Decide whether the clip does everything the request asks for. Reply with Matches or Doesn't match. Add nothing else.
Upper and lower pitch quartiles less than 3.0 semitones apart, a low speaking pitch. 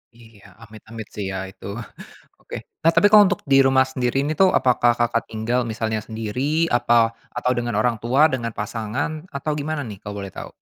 Doesn't match